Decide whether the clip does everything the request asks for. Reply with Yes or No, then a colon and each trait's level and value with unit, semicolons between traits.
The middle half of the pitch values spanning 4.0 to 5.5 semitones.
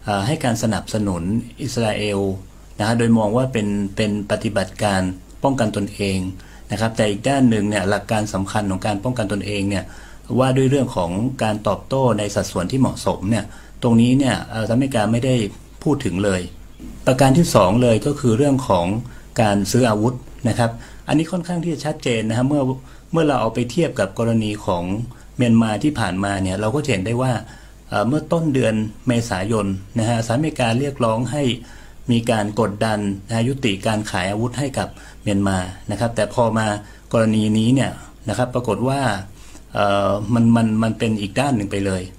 No: average, 3.6 semitones